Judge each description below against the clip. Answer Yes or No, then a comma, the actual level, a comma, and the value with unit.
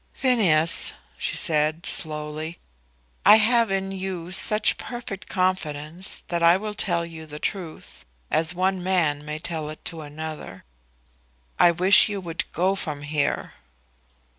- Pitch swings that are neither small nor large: Yes, average, 3.7 semitones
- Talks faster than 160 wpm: No, average, 140 wpm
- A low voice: No, medium, 170 Hz